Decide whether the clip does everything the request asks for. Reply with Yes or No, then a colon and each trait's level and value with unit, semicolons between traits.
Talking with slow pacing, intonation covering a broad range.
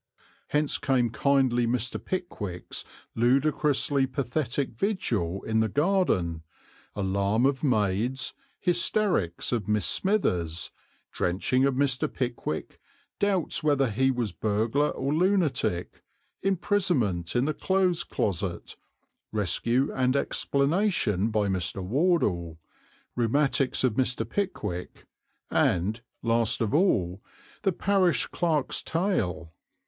Yes: slow, 105 wpm; wide, 6.8 semitones